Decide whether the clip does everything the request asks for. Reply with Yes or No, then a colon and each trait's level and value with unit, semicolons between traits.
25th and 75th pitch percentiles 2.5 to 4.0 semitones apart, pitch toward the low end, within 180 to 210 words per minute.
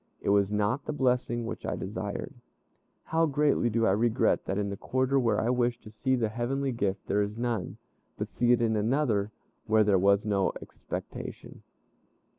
Yes: average, 3.4 semitones; low, 115 Hz; average, 185 wpm